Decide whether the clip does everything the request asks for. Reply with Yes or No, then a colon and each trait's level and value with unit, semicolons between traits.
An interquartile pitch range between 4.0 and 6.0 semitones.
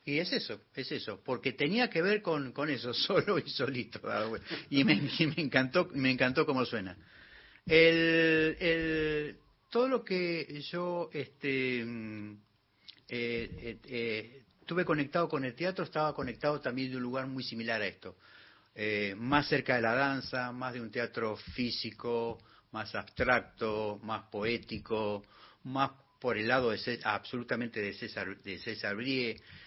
Yes: average, 5.3 semitones